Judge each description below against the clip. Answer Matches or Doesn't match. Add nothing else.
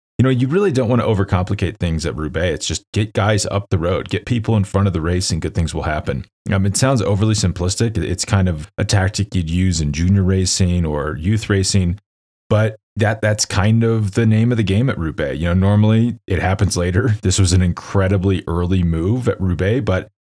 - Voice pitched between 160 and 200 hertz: Doesn't match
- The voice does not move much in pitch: Doesn't match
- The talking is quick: Matches